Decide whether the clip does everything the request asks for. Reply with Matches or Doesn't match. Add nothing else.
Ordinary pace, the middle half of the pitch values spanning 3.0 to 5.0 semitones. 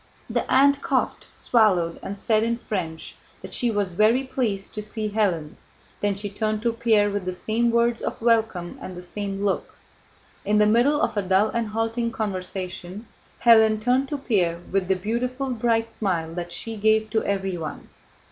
Matches